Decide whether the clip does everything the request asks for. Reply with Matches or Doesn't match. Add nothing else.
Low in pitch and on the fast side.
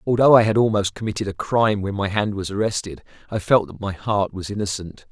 Matches